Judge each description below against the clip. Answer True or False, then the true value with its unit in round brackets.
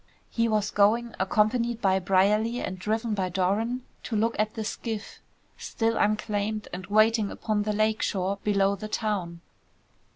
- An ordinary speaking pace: True (155 wpm)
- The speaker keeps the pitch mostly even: True (2.1 semitones)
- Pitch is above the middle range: True (215 Hz)